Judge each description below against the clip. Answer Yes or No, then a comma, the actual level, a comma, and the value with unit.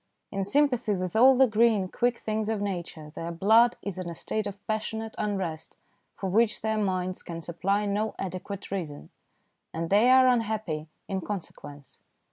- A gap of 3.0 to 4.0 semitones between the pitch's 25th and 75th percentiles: Yes, average, 3.4 semitones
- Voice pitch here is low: No, high, 200 Hz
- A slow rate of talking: No, average, 165 wpm